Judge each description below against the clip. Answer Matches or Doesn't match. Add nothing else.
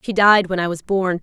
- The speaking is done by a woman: Matches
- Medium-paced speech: Doesn't match